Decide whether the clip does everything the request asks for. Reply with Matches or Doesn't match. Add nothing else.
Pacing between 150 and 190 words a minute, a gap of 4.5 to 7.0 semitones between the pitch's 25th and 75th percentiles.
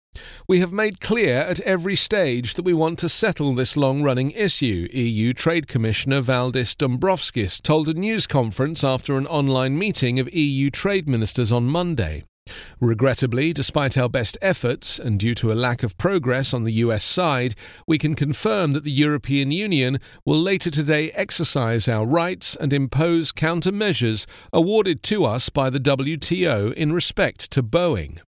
Matches